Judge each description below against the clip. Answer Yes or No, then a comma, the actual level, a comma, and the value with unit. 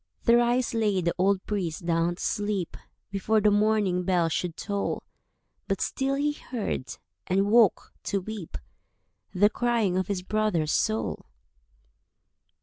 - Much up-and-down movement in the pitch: No, average, 3.5 semitones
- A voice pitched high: Yes, high, 200 Hz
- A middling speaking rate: No, slow, 130 wpm